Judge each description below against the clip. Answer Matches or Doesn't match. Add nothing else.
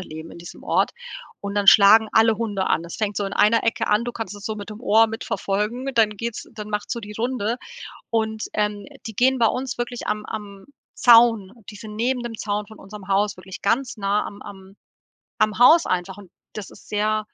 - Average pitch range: Doesn't match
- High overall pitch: Matches